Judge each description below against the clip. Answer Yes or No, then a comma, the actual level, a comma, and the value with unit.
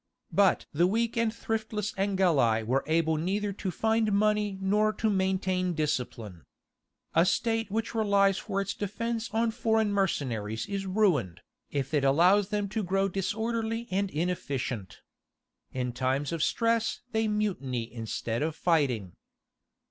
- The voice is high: Yes, high, 195 Hz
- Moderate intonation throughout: No, wide, 6.6 semitones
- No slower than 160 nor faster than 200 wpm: No, average, 140 wpm